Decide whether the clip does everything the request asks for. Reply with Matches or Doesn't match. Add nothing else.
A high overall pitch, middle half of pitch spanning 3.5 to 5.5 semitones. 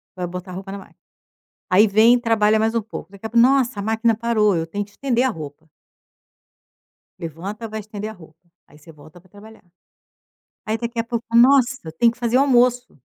Matches